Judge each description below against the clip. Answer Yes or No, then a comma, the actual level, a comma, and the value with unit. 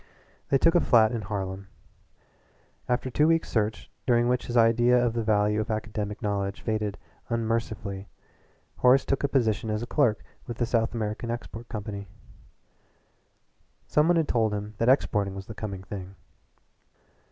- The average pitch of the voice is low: Yes, low, 110 Hz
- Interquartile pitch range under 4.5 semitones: Yes, narrow, 2.6 semitones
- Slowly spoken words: No, average, 155 wpm